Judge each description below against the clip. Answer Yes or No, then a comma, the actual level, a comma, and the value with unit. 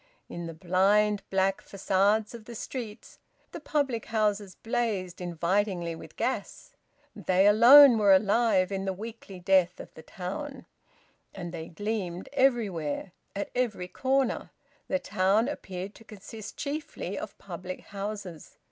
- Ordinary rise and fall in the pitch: Yes, average, 3.8 semitones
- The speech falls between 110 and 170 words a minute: Yes, slow, 135 wpm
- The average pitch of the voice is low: No, high, 200 Hz